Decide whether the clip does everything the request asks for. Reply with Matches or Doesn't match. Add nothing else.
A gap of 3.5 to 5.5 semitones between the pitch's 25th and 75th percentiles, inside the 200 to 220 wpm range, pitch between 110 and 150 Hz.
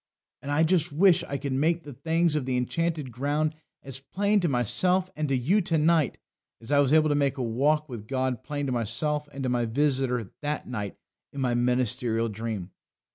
Matches